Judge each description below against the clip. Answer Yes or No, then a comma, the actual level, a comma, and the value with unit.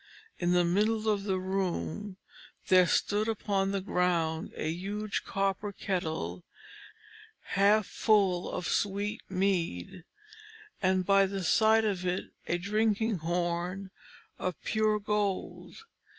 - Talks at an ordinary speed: No, slow, 120 wpm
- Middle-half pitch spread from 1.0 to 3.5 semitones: Yes, average, 2.7 semitones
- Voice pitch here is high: Yes, high, 195 Hz